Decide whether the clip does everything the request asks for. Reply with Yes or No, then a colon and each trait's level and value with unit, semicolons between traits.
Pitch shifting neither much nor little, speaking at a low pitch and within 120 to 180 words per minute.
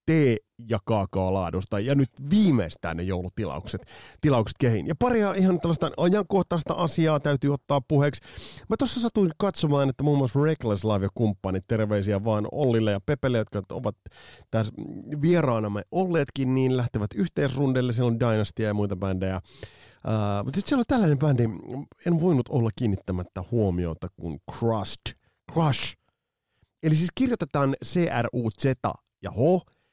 No: wide, 7.0 semitones; low, 125 Hz; average, 140 wpm